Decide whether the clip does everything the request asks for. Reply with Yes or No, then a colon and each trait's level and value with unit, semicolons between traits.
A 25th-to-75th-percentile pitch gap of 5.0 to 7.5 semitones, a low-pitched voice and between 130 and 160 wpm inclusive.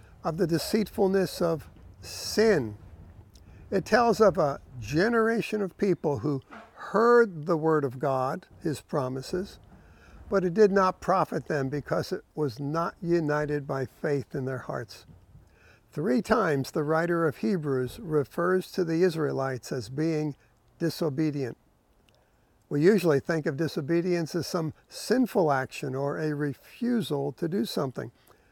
No: wide, 5.6 semitones; medium, 155 Hz; slow, 135 wpm